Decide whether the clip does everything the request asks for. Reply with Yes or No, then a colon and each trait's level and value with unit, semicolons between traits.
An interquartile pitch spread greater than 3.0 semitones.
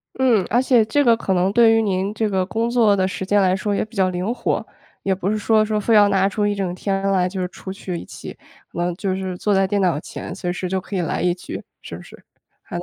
No: narrow, 2.6 semitones